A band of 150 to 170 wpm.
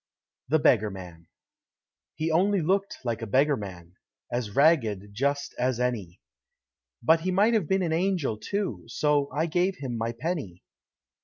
Yes: average, 155 wpm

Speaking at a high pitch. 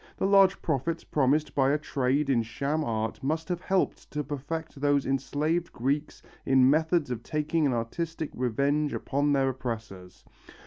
No: medium, 145 Hz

